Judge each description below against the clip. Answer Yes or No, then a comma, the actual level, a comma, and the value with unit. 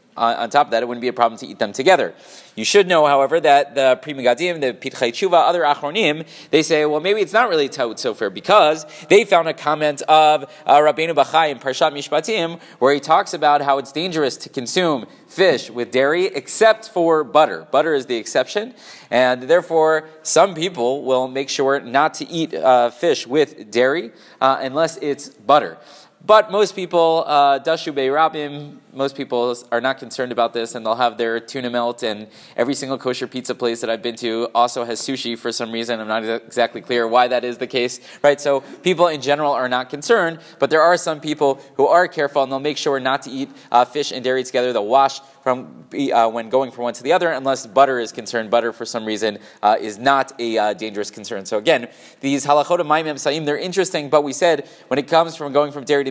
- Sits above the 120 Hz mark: Yes, medium, 140 Hz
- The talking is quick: Yes, fast, 215 wpm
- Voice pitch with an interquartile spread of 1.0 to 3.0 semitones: No, average, 4.3 semitones